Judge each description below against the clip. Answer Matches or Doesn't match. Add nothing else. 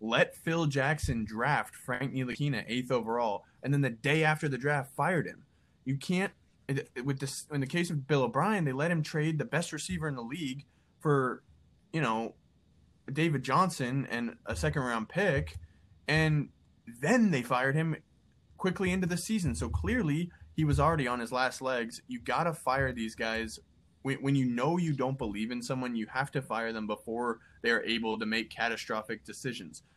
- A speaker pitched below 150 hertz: Matches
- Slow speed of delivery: Doesn't match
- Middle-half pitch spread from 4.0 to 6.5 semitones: Matches